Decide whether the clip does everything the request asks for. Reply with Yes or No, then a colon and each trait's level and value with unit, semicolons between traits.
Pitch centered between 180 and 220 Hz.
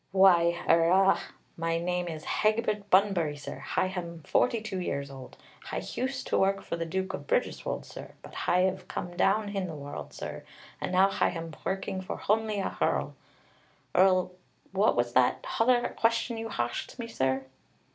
Yes: medium, 185 Hz